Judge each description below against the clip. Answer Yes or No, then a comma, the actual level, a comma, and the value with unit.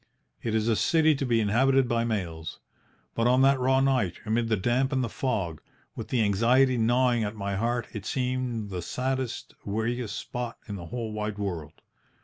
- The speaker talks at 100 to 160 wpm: No, average, 185 wpm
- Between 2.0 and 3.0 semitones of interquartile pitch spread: No, average, 3.4 semitones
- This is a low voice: Yes, low, 115 Hz